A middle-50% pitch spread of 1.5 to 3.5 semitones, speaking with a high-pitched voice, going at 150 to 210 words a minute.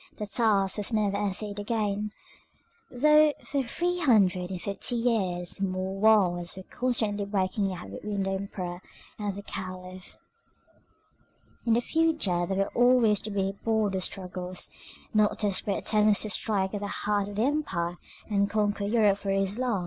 Yes: narrow, 2.4 semitones; high, 205 Hz; average, 155 wpm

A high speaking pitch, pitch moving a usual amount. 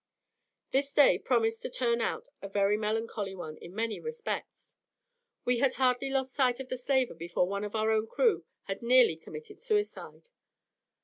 Yes: high, 235 Hz; average, 4.4 semitones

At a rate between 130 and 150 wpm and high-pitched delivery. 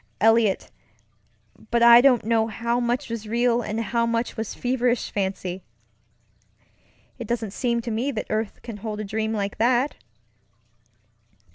Yes: average, 145 wpm; high, 230 Hz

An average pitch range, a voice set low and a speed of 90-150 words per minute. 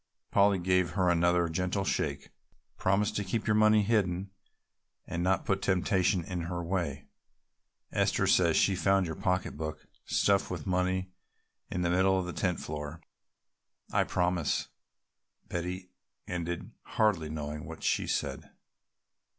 No: narrow, 2.0 semitones; very low, 90 Hz; slow, 135 wpm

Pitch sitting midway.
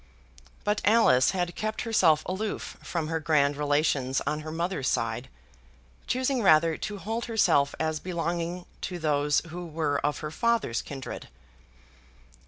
Yes: medium, 160 Hz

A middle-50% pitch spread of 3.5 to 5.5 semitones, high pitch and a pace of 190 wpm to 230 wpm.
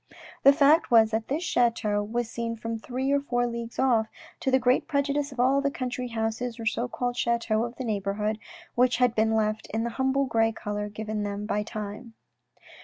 No: narrow, 2.6 semitones; high, 235 Hz; average, 200 wpm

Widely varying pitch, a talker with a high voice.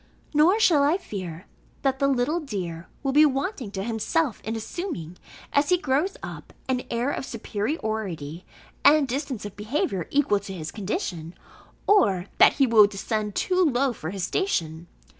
Yes: wide, 7.1 semitones; high, 235 Hz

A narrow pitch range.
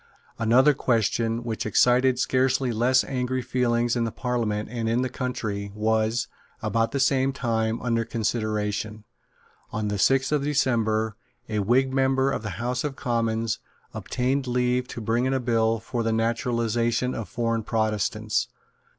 Yes: narrow, 2.3 semitones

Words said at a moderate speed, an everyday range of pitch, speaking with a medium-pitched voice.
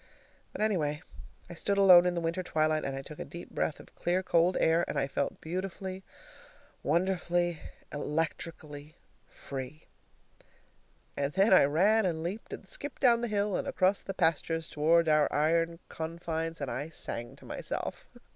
Yes: average, 165 wpm; average, 3.3 semitones; medium, 165 Hz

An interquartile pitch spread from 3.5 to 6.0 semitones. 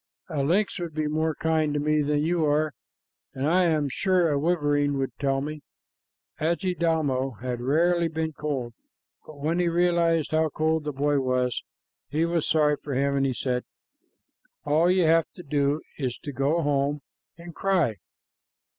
No: average, 2.9 semitones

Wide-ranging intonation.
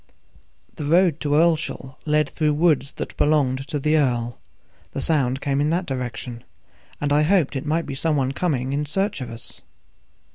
No: average, 2.8 semitones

